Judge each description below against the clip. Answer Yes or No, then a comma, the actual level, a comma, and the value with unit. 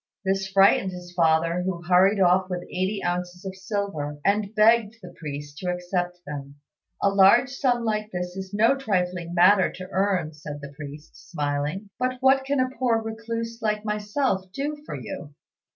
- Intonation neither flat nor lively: Yes, average, 3.4 semitones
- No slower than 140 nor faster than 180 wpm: Yes, average, 170 wpm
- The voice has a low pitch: No, high, 190 Hz